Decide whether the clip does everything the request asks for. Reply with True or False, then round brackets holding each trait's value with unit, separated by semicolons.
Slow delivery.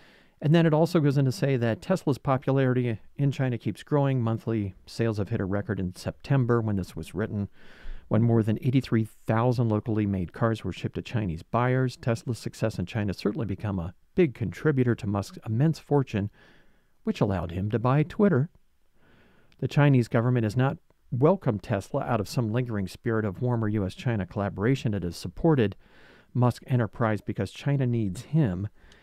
False (175 wpm)